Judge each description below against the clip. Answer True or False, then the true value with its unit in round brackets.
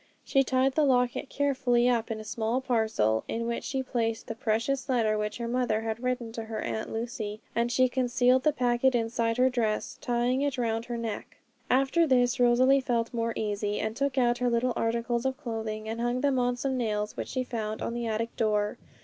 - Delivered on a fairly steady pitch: True (2.2 semitones)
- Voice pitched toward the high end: True (240 Hz)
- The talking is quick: True (210 wpm)